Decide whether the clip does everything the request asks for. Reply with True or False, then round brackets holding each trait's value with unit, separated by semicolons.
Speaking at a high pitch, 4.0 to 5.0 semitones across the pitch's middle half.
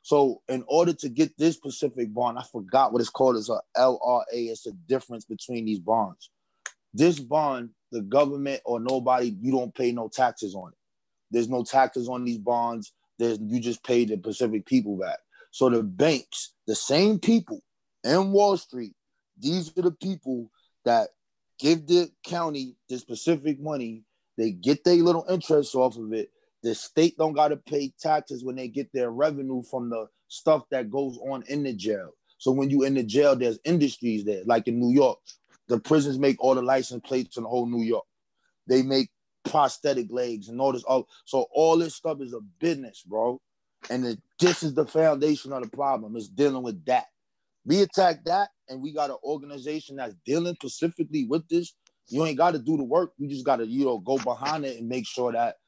False (135 Hz; 4.3 semitones)